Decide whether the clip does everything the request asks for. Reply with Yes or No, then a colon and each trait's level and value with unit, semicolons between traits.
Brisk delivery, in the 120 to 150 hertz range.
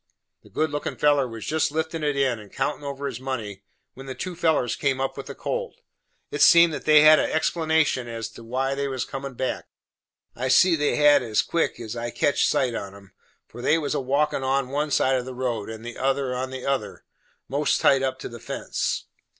Yes: fast, 225 wpm; low, 135 Hz